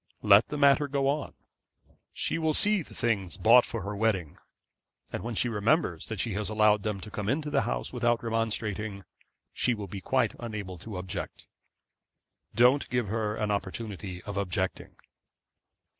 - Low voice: Yes, low, 110 Hz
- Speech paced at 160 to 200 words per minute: Yes, average, 165 wpm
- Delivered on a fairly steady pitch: No, average, 3.4 semitones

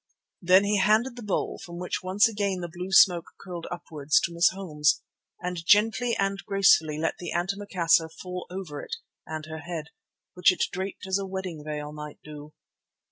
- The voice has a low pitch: No, medium, 180 Hz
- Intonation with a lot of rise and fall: No, average, 3.4 semitones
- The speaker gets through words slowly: No, average, 180 wpm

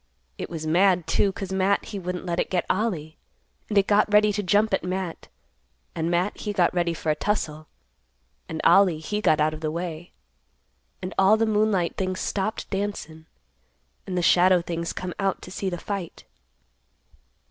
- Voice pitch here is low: No, medium, 185 Hz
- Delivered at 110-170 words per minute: No, average, 180 wpm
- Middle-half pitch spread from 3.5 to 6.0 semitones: No, average, 3.0 semitones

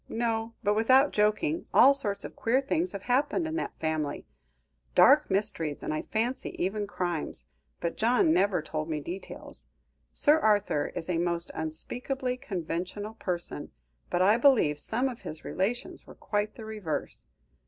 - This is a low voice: No, high, 210 Hz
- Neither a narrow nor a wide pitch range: No, wide, 6.3 semitones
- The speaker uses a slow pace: No, average, 155 wpm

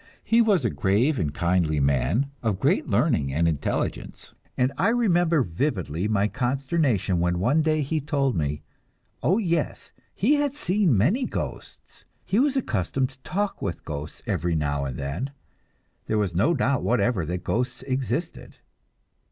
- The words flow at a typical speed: Yes, average, 155 wpm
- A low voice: Yes, low, 125 Hz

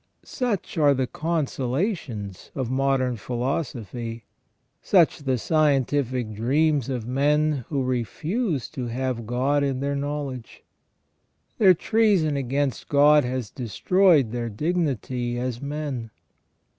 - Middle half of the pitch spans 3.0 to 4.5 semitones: Yes, average, 3.6 semitones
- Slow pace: Yes, slow, 115 wpm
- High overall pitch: No, low, 135 Hz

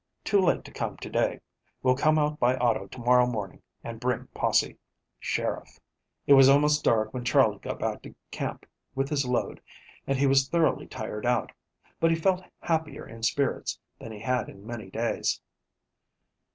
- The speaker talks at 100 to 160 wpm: No, average, 180 wpm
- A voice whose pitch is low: Yes, low, 130 Hz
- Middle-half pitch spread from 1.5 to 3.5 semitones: No, average, 4.1 semitones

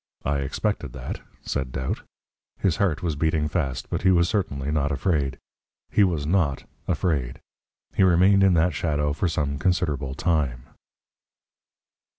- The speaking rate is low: No, average, 145 wpm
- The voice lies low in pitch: Yes, very low, 75 Hz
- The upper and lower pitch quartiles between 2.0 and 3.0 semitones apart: No, average, 4.2 semitones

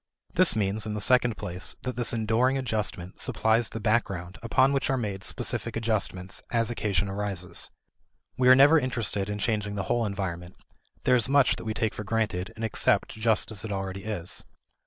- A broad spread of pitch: No, average, 3.3 semitones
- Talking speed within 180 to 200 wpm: Yes, average, 185 wpm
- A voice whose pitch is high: No, low, 110 Hz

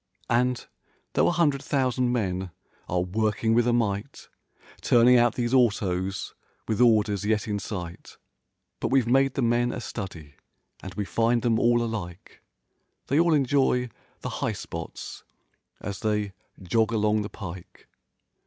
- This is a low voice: Yes, low, 115 Hz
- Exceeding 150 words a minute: No, average, 145 wpm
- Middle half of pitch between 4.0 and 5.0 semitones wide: No, average, 3.5 semitones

